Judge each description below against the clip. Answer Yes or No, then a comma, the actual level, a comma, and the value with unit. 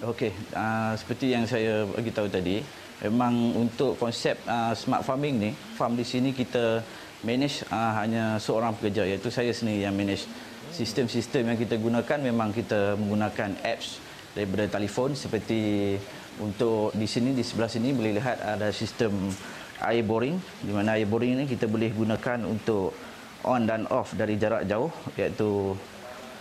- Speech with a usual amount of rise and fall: No, narrow, 2.2 semitones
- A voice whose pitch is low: Yes, low, 115 Hz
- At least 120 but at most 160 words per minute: Yes, fast, 155 wpm